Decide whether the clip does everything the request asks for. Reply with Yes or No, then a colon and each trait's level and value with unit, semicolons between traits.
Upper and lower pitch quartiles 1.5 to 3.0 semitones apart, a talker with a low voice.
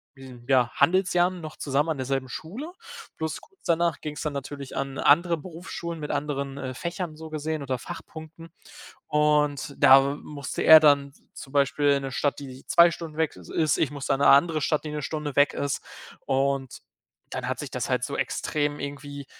No: narrow, 2.5 semitones; medium, 145 Hz